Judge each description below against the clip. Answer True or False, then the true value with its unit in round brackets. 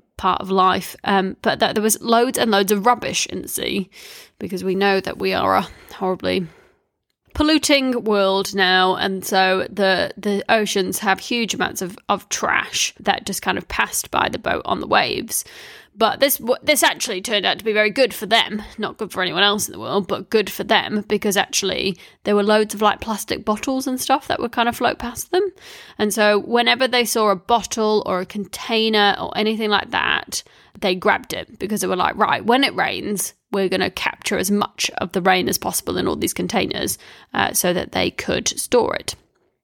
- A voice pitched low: False (210 Hz)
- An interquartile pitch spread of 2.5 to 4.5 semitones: True (3.4 semitones)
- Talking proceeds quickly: True (210 wpm)